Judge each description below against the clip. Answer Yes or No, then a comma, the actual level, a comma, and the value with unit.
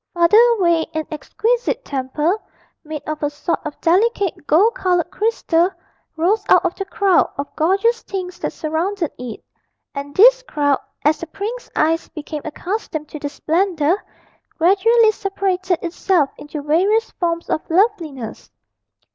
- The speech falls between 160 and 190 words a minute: No, average, 140 wpm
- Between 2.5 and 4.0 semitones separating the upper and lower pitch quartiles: No, average, 4.5 semitones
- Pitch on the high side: Yes, very high, 345 Hz